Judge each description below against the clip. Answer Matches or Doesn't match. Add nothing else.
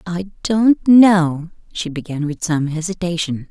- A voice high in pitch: Doesn't match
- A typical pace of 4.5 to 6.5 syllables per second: Doesn't match